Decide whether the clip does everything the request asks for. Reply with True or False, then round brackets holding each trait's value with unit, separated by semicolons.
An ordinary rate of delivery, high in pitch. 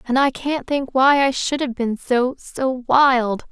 True (190 wpm; 260 Hz)